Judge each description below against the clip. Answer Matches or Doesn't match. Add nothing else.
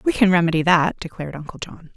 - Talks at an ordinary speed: Doesn't match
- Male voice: Doesn't match